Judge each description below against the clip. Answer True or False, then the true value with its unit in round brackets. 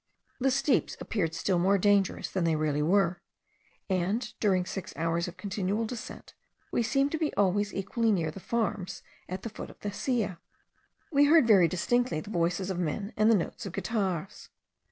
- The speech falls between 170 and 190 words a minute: True (180 wpm)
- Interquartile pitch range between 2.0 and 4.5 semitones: True (4.1 semitones)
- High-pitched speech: True (195 Hz)